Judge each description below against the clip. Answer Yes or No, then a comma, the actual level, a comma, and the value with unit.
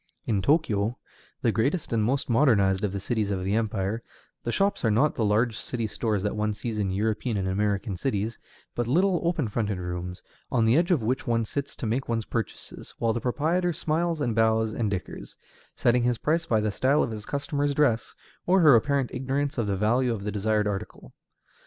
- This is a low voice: Yes, low, 115 Hz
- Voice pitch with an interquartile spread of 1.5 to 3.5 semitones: No, average, 4.9 semitones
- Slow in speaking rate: No, fast, 205 wpm